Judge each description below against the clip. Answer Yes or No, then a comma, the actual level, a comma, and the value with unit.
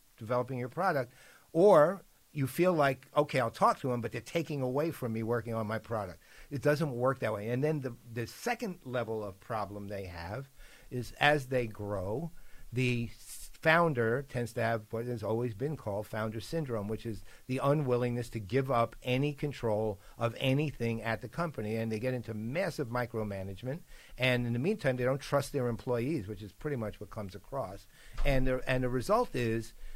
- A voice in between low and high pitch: No, low, 125 Hz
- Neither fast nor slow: Yes, average, 190 wpm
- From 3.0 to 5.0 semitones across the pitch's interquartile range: Yes, average, 3.5 semitones